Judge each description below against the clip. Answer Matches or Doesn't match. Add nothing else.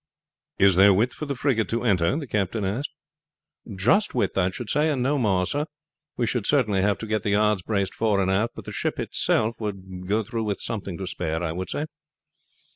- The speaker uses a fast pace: Matches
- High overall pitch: Doesn't match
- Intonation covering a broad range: Doesn't match